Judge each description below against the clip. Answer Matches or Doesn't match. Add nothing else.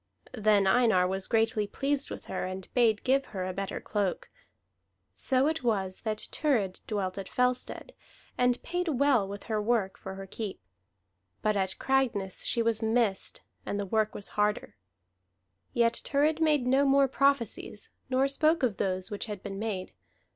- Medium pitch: Doesn't match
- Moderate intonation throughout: Matches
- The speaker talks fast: Doesn't match